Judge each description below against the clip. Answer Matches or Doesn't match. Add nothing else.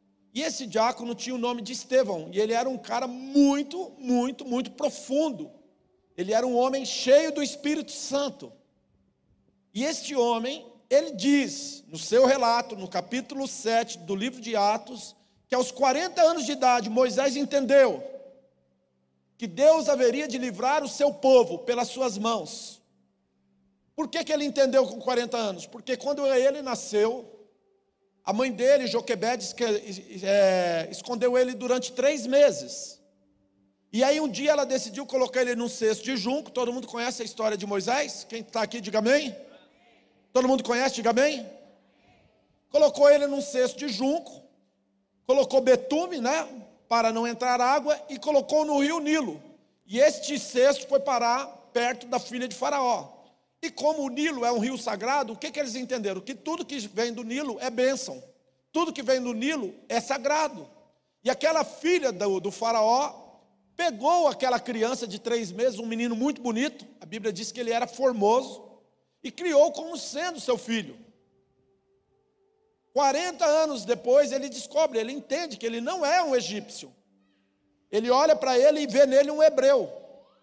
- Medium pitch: Doesn't match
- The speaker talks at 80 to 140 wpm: Doesn't match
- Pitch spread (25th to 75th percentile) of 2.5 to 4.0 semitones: Matches